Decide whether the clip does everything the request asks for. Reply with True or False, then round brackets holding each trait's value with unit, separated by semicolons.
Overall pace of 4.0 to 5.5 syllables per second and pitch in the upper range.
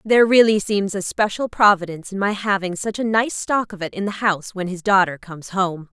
False (5.7 syllables/s; 195 Hz)